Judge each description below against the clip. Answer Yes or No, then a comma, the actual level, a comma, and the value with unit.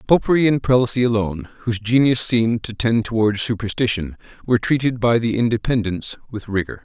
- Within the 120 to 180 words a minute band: Yes, average, 160 wpm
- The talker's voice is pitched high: No, low, 115 Hz